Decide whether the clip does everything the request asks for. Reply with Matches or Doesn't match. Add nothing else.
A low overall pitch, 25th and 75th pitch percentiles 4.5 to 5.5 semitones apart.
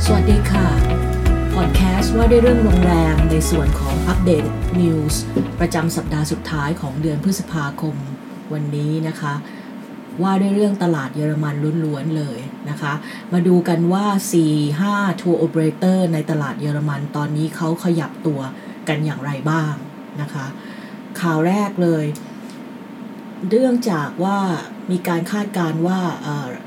Doesn't match